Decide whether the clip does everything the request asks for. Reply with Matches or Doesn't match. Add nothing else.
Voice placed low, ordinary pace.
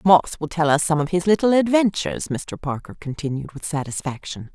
Doesn't match